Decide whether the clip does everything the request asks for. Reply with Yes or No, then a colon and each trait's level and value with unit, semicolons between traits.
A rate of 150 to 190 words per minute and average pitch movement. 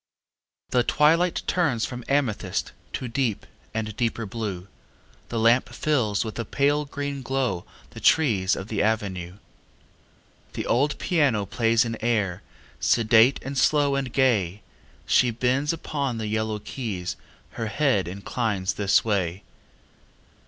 No: slow, 135 wpm; average, 4.7 semitones